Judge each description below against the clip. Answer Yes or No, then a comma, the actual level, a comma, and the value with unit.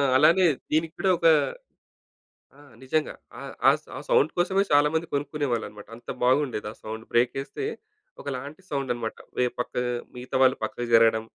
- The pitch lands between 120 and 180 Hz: Yes, low, 135 Hz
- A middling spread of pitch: Yes, average, 4.2 semitones